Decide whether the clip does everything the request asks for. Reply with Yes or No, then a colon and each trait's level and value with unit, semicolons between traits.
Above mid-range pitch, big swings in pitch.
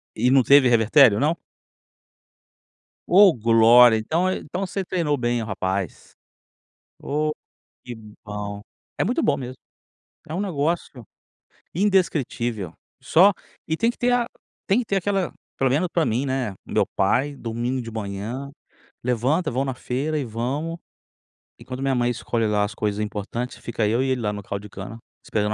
No: low, 125 Hz; wide, 6.0 semitones